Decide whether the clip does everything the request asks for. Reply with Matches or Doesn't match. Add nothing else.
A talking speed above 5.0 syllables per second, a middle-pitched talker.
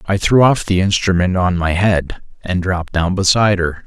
Doesn't match